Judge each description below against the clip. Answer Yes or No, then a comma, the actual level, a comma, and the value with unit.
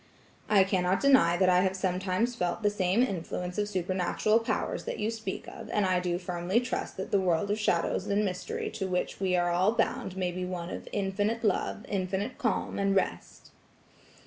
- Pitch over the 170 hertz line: Yes, high, 190 Hz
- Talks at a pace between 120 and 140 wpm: No, average, 195 wpm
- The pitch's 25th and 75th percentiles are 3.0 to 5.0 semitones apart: No, narrow, 2.5 semitones